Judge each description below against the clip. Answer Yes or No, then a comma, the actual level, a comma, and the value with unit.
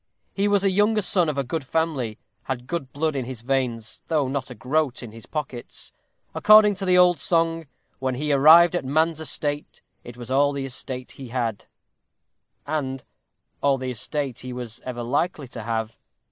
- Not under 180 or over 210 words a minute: Yes, average, 185 wpm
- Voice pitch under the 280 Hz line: Yes, medium, 140 Hz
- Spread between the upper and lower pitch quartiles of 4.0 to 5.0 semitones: Yes, average, 4.5 semitones